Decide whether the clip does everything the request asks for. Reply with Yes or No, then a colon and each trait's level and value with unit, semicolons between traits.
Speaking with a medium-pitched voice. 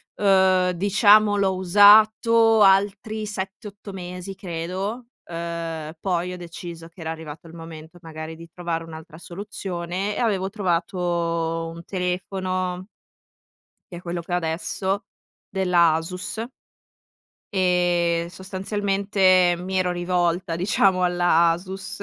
Yes: medium, 180 Hz